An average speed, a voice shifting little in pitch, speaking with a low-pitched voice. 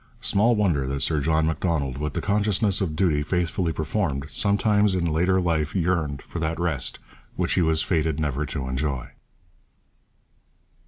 No: average, 155 wpm; average, 4.0 semitones; very low, 80 Hz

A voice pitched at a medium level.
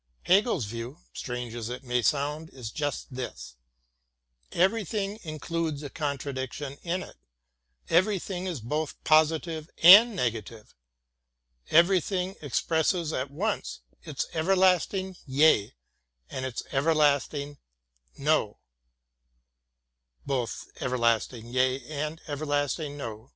Yes: medium, 155 Hz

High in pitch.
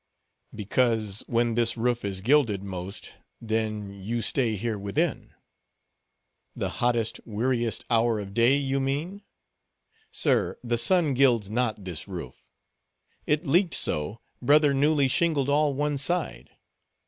No: low, 120 Hz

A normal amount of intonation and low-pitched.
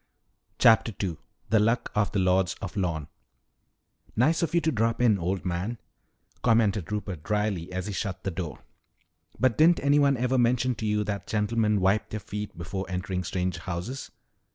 Yes: average, 3.9 semitones; low, 105 Hz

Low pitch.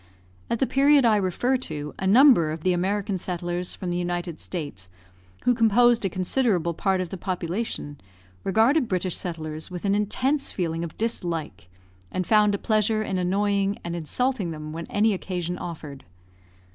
No: medium, 185 Hz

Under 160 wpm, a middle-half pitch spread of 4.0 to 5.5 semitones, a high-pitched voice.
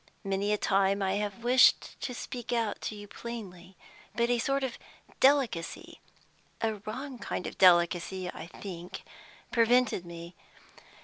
Yes: average, 140 wpm; average, 4.5 semitones; high, 205 Hz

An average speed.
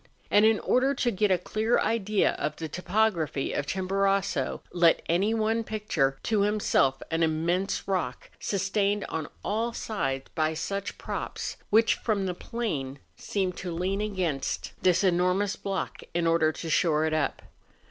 Yes: average, 155 wpm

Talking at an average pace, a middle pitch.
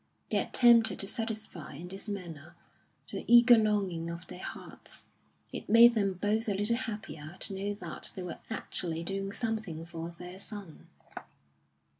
No: average, 155 wpm; high, 195 Hz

